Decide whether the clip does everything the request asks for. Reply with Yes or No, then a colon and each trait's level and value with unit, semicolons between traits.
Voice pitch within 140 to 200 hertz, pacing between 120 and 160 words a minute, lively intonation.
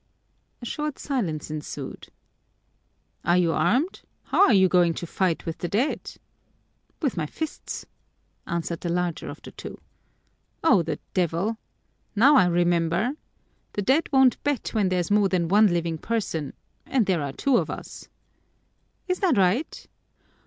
Yes: medium, 185 Hz; average, 150 wpm; wide, 6.4 semitones